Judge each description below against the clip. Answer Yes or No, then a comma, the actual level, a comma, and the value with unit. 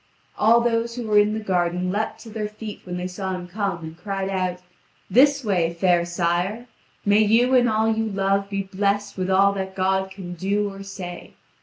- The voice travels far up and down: No, average, 2.8 semitones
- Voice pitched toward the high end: Yes, high, 195 Hz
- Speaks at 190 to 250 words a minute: Yes, average, 200 wpm